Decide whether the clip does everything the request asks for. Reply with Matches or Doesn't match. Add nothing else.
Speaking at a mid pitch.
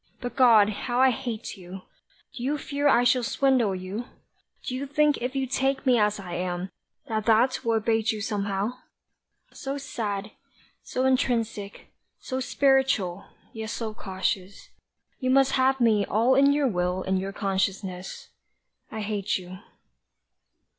Doesn't match